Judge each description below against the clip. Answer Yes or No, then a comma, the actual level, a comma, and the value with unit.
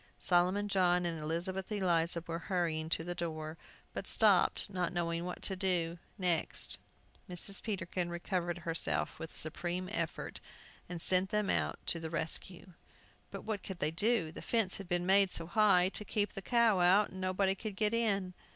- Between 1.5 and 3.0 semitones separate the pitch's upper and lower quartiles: Yes, narrow, 2.6 semitones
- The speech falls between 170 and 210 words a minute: Yes, average, 180 wpm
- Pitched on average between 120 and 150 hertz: No, medium, 180 Hz